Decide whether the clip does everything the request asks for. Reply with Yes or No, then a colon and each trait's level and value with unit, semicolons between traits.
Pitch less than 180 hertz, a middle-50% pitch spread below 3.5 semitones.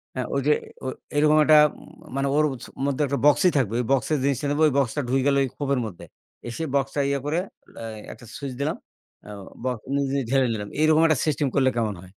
Yes: medium, 140 Hz; narrow, 2.6 semitones